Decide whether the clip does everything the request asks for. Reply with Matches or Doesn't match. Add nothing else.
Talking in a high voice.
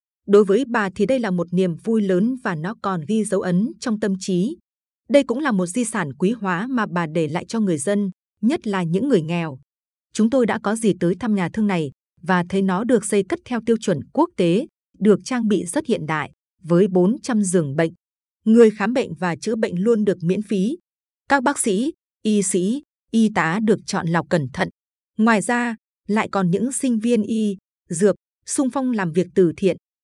Matches